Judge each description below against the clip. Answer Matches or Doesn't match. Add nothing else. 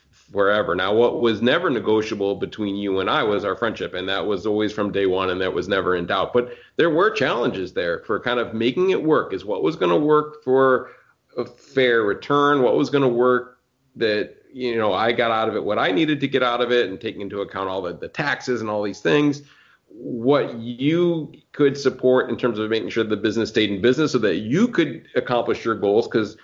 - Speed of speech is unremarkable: Doesn't match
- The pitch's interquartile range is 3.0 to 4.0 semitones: Matches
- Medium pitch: Doesn't match